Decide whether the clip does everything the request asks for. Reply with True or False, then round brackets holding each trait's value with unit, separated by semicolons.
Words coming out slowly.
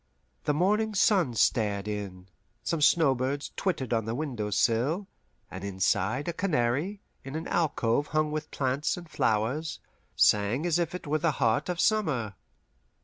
False (150 wpm)